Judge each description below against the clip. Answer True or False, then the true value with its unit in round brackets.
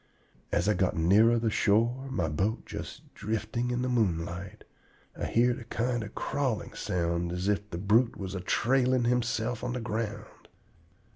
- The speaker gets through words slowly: False (165 wpm)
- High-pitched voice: False (110 Hz)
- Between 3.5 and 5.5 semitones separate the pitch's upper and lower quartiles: True (4.2 semitones)